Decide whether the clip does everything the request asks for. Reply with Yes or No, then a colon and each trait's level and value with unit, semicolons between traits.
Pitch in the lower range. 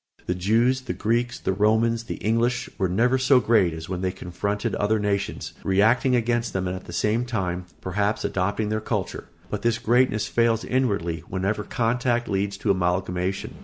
Yes: low, 105 Hz